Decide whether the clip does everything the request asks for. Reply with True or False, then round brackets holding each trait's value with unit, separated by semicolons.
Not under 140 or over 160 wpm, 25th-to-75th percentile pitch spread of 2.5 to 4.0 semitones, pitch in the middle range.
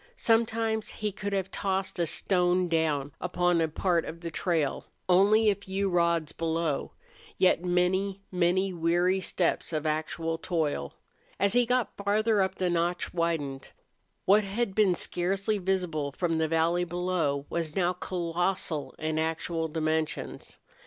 True (145 wpm; 2.9 semitones; 175 Hz)